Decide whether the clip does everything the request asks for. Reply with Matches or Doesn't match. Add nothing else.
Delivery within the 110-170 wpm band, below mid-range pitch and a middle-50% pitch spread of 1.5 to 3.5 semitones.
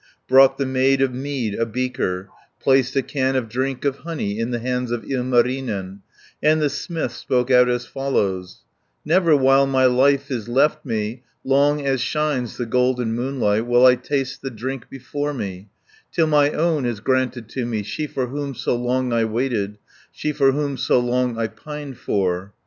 Doesn't match